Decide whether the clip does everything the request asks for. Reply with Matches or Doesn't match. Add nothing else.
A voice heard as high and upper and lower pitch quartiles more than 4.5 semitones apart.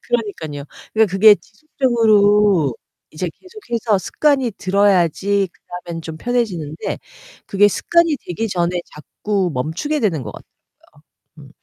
Matches